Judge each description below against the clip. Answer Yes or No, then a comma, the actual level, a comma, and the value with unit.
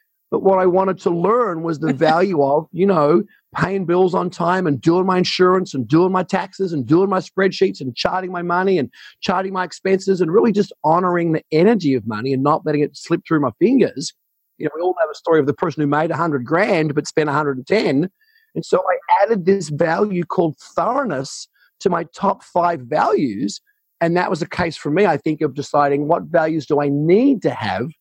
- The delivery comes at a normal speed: No, fast, 220 wpm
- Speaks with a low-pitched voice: No, medium, 175 Hz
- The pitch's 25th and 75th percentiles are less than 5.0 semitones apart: Yes, average, 3.7 semitones